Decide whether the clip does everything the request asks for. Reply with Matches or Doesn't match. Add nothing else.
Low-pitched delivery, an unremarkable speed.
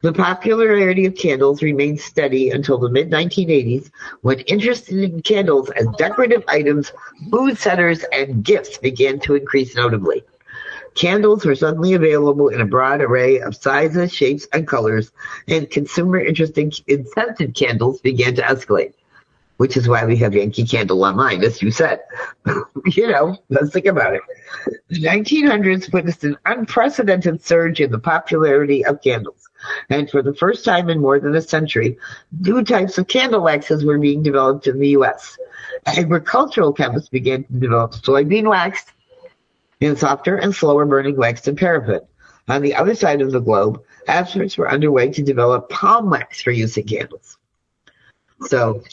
Doesn't match